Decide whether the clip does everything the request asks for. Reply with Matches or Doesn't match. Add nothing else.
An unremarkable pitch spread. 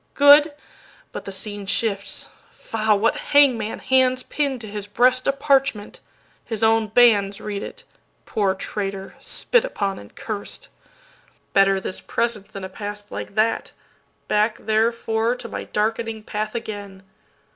Matches